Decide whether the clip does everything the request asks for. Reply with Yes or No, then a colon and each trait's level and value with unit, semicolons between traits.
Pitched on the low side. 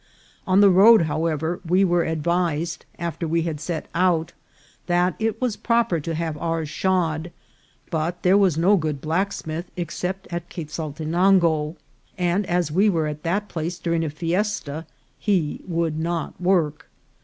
No: medium, 170 Hz